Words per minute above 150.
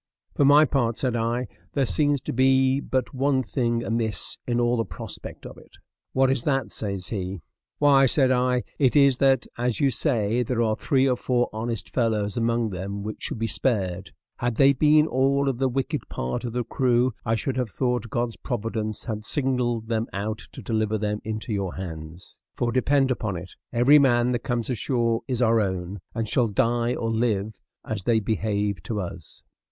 Yes: average, 190 wpm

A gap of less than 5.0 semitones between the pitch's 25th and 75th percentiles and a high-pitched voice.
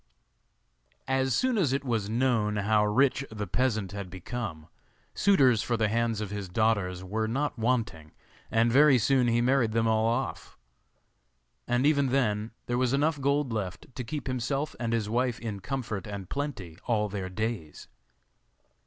No: average, 3.9 semitones; low, 115 Hz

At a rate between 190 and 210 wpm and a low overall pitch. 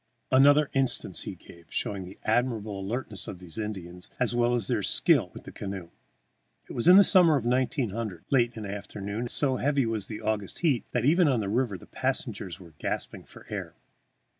Yes: average, 200 wpm; low, 115 Hz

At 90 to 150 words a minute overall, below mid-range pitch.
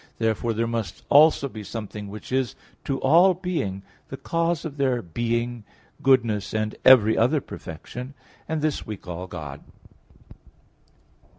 Yes: slow, 135 wpm; low, 120 Hz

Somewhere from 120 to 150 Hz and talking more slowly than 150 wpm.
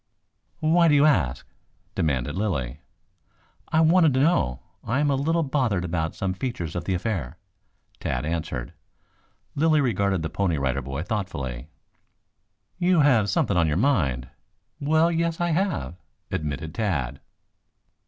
No: very low, 95 Hz; average, 140 wpm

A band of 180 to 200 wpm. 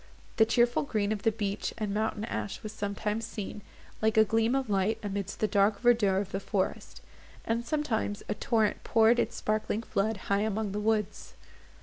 Yes: average, 185 wpm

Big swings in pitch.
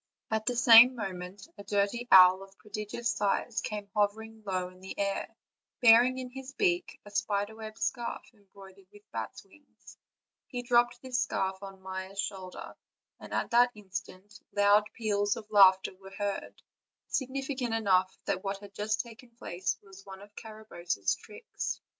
No: average, 3.3 semitones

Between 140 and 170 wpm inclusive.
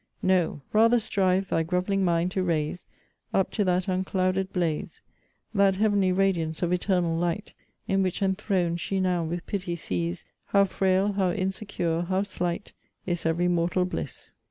Yes: average, 155 wpm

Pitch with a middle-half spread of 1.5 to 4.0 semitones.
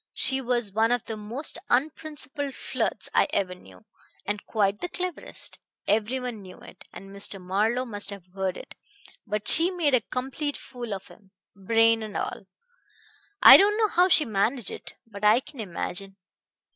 No: average, 4.9 semitones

